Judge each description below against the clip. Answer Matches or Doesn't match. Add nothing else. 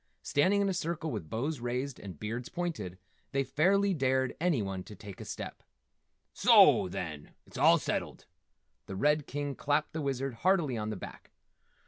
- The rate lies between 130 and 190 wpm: Matches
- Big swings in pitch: Matches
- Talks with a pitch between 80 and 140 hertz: Matches